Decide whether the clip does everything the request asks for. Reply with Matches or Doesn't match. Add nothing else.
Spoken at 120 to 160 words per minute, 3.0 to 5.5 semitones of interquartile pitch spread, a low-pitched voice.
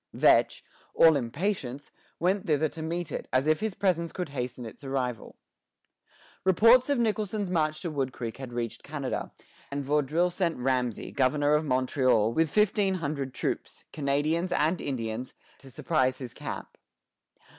Doesn't match